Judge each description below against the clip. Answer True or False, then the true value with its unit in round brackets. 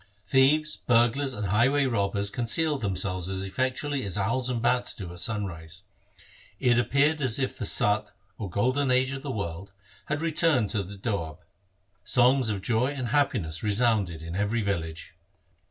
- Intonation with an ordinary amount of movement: True (4.9 semitones)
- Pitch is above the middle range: False (115 Hz)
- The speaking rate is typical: True (160 wpm)